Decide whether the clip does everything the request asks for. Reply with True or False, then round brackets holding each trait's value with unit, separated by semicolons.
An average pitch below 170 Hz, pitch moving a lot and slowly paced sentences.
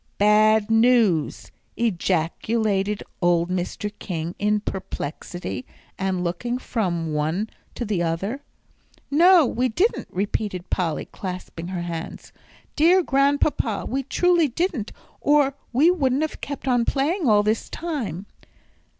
False (215 Hz; 7.1 semitones; 120 wpm)